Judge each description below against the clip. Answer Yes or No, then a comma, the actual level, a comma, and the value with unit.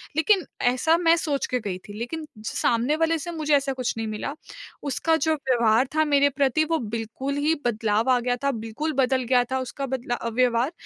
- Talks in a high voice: Yes, very high, 265 Hz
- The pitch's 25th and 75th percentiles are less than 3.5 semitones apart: No, average, 4.7 semitones